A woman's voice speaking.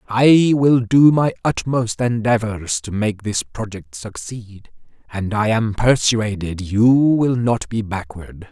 No: male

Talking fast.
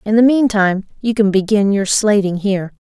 No: average, 190 wpm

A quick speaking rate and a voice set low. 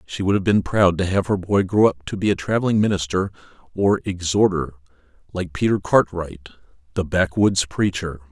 No: average, 175 wpm; very low, 90 Hz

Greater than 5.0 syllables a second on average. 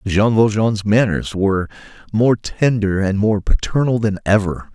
No: 4.4 syllables/s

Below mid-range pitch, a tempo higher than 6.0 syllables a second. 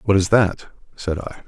No: very low, 95 Hz; 4.3 syllables/s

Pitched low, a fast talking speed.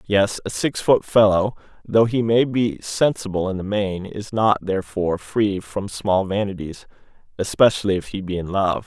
No: low, 100 Hz; average, 175 wpm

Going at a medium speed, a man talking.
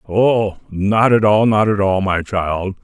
Yes: average, 190 wpm; male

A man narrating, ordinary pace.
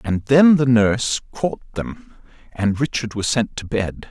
Yes: male; average, 175 wpm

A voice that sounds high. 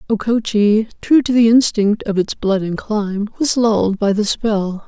Yes: high, 215 Hz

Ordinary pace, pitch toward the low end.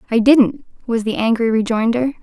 No: average, 160 wpm; high, 235 Hz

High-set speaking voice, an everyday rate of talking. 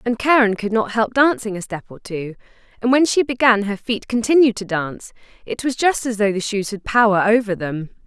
No: high, 220 Hz; fast, 225 wpm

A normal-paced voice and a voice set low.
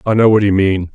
No: fast, 320 wpm; low, 100 Hz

